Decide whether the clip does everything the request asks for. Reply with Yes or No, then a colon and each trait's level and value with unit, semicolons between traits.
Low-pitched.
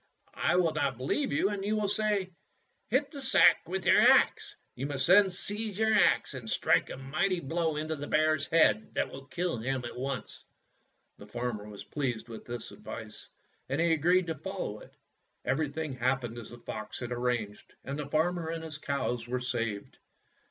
No: medium, 145 Hz